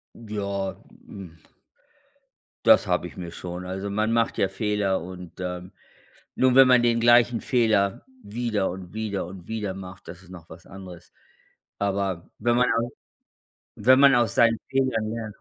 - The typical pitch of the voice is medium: No, low, 100 Hz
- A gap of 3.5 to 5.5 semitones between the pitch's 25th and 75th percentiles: Yes, average, 4.0 semitones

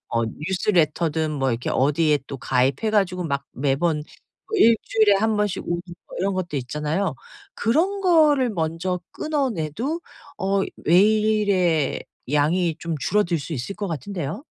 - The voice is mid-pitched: Yes, medium, 175 Hz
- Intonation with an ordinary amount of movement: No, wide, 5.8 semitones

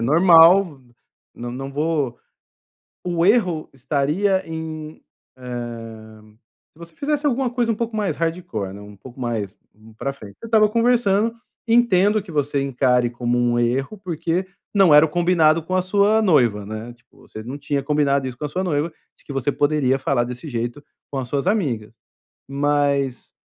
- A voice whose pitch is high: No, medium, 145 Hz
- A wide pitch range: Yes, wide, 7.0 semitones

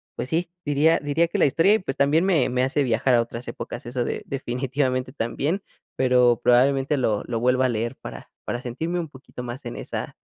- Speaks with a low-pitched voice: Yes, low, 130 Hz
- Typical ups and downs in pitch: Yes, average, 3.1 semitones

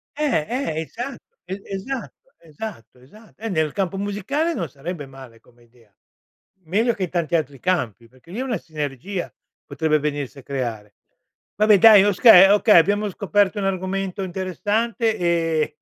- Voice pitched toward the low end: No, medium, 185 Hz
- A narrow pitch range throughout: No, wide, 6.0 semitones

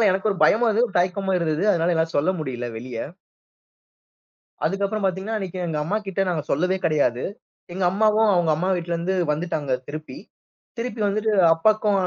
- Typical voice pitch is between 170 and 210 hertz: Yes, medium, 185 Hz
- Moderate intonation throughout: Yes, average, 4.4 semitones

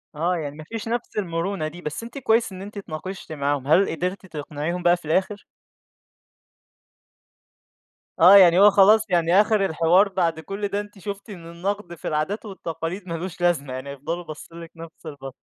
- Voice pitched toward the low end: No, medium, 175 Hz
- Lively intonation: No, average, 3.8 semitones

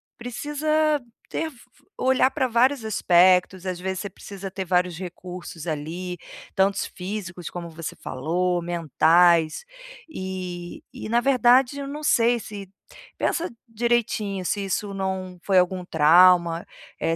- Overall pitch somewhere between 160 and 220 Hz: Yes, high, 190 Hz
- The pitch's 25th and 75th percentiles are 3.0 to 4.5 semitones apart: No, average, 5.1 semitones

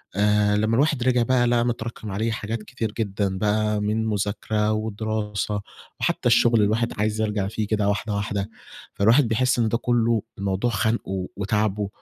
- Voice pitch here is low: Yes, low, 110 Hz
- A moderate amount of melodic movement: No, narrow, 2.0 semitones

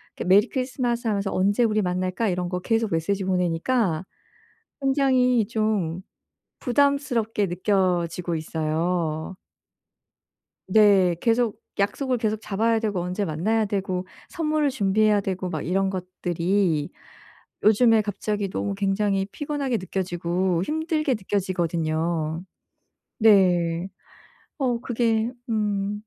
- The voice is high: Yes, high, 200 Hz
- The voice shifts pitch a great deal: No, average, 3.9 semitones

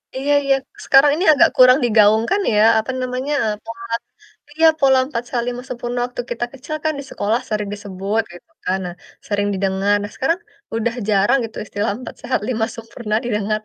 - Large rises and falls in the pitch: No, average, 3.7 semitones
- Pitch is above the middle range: Yes, high, 230 Hz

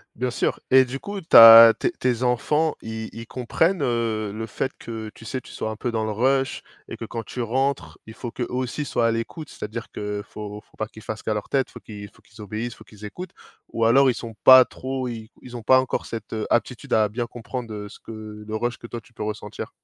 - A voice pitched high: No, low, 115 Hz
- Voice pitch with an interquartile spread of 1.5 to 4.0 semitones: Yes, average, 2.8 semitones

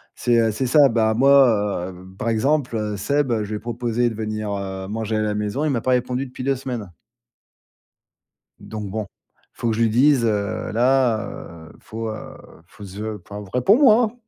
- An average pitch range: Yes, average, 3.3 semitones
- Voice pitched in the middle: No, low, 110 Hz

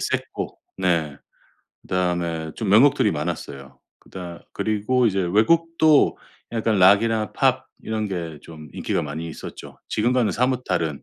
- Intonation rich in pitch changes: Yes, wide, 5.7 semitones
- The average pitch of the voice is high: No, very low, 95 Hz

